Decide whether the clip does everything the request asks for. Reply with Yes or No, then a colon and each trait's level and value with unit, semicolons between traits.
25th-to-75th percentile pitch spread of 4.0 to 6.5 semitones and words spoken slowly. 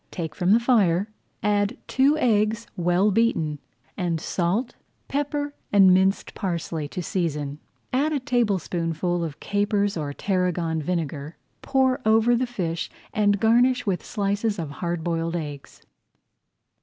Yes: average, 5.2 semitones; slow, 130 wpm